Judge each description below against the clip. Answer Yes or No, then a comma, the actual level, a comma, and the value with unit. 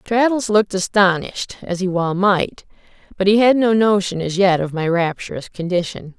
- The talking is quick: No, average, 175 wpm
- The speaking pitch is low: No, high, 190 Hz